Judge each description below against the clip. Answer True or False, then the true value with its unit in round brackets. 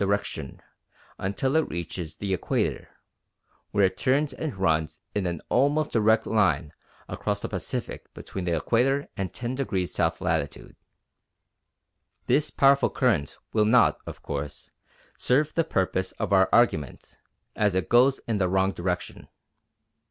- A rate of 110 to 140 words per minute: True (135 wpm)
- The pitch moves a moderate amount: False (6.2 semitones)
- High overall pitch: False (100 Hz)